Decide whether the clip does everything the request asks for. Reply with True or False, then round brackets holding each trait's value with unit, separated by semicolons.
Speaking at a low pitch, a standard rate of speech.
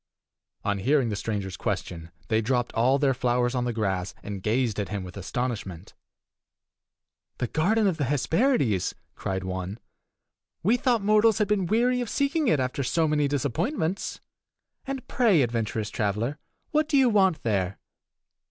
True (130 Hz; 155 wpm)